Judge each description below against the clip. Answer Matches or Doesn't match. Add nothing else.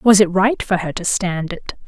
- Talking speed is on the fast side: Matches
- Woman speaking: Matches